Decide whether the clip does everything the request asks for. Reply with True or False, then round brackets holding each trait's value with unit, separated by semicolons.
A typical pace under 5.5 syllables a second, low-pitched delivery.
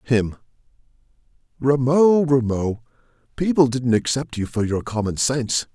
True (4.5 syllables/s; 130 Hz)